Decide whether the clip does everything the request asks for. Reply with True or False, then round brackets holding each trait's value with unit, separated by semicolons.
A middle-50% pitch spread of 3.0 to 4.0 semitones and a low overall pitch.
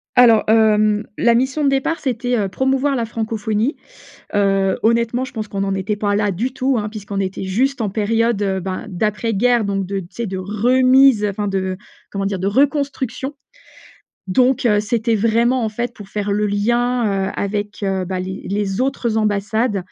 False (3.5 semitones; 215 Hz)